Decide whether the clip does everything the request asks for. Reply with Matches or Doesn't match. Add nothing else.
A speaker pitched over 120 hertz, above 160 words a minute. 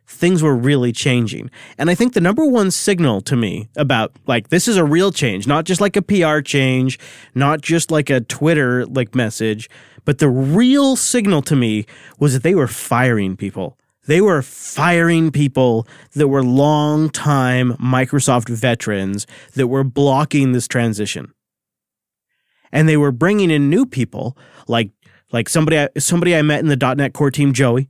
Matches